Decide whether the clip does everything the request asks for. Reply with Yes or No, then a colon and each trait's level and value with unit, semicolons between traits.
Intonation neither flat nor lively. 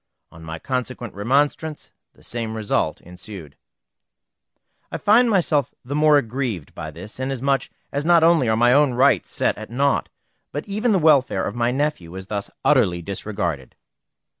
No: wide, 6.3 semitones